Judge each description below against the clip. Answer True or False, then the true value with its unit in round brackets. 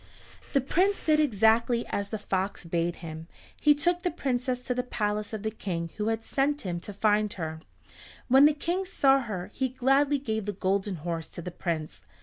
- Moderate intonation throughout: False (6.4 semitones)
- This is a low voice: False (220 Hz)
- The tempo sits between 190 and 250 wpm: True (195 wpm)